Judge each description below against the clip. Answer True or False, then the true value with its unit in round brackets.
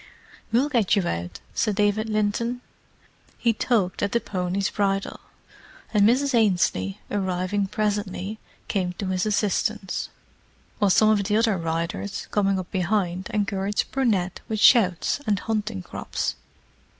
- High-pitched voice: True (205 Hz)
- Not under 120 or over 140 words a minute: True (135 wpm)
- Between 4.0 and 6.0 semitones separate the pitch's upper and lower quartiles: False (2.7 semitones)